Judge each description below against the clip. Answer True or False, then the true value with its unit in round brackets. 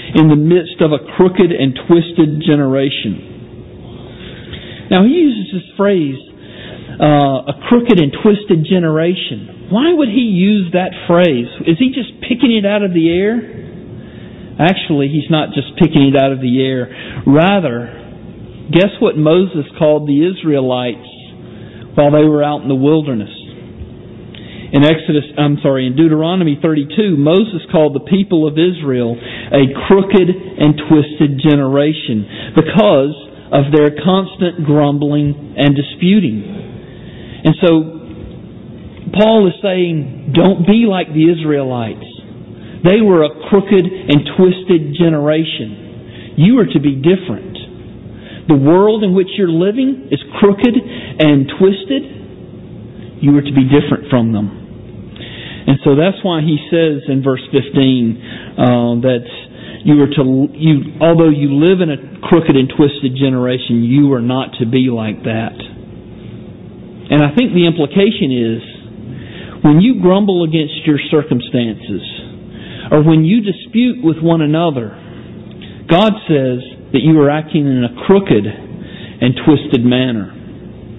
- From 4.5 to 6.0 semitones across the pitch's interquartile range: True (5.1 semitones)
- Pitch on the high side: False (150 Hz)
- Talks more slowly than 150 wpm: True (135 wpm)